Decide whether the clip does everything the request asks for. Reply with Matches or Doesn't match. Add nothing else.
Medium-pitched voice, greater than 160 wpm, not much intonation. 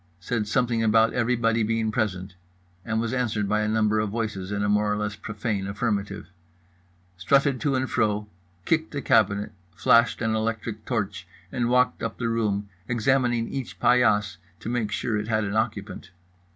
Doesn't match